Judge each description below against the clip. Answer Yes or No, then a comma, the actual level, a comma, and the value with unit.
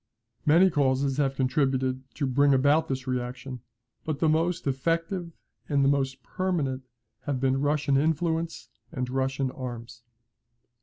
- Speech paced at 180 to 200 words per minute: No, slow, 135 wpm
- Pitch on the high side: No, low, 135 Hz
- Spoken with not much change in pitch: No, average, 3.0 semitones